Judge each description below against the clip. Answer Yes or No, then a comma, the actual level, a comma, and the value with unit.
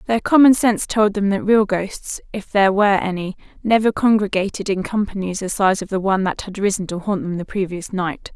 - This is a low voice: No, high, 200 Hz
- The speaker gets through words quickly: Yes, fast, 215 wpm